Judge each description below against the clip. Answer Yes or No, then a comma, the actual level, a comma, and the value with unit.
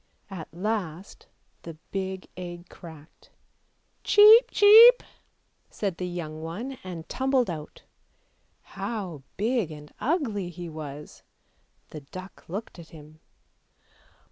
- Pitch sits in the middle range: Yes, medium, 180 Hz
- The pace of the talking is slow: Yes, slow, 110 wpm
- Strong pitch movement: Yes, wide, 5.7 semitones